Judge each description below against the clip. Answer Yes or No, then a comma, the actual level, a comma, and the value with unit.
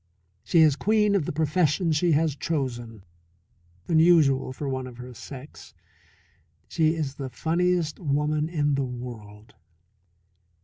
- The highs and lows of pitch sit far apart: No, average, 3.9 semitones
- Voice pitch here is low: No, medium, 150 Hz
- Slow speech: Yes, slow, 130 wpm